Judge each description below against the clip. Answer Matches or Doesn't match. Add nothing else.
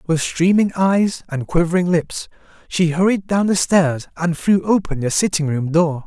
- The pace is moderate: Matches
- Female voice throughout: Doesn't match